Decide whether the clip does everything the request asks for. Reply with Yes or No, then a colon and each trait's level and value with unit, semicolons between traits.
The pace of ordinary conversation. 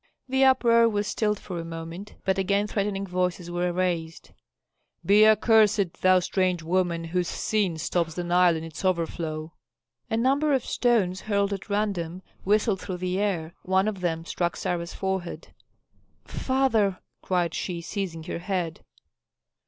Yes: average, 150 wpm